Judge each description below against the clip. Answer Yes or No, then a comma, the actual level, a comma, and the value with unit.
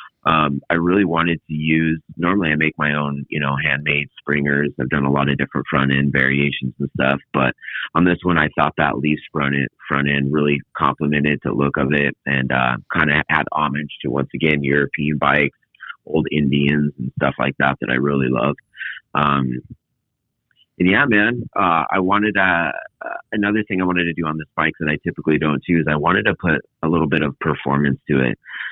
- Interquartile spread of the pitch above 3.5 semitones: No, narrow, 2.5 semitones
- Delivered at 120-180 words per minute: No, fast, 205 wpm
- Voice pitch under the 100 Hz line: Yes, very low, 75 Hz